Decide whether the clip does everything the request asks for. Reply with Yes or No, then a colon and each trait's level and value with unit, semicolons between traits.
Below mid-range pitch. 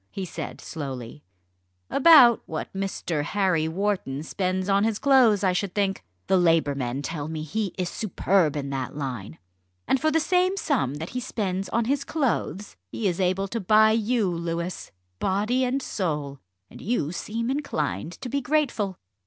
No: high, 195 Hz